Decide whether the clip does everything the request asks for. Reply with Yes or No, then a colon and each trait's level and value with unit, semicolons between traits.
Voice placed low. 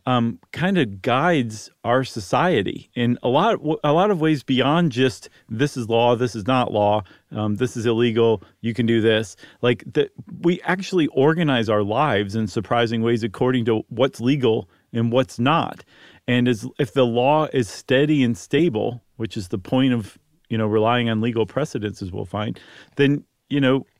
Yes: low, 120 Hz